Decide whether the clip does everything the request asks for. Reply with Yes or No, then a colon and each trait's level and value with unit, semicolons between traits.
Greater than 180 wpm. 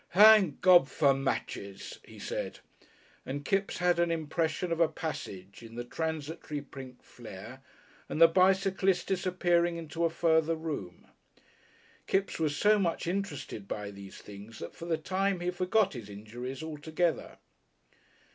No: average, 145 wpm